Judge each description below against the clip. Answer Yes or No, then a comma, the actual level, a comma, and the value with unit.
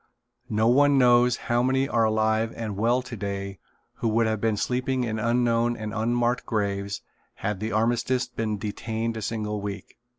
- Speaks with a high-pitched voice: No, low, 115 Hz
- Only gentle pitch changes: Yes, narrow, 2.2 semitones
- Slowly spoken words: No, average, 165 wpm